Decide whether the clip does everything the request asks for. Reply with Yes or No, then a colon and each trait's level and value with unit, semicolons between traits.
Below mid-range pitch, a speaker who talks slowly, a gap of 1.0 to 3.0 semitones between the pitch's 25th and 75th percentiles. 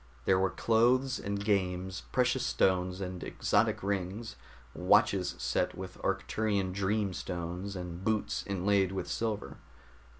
Yes: low, 100 Hz; slow, 125 wpm; narrow, 2.6 semitones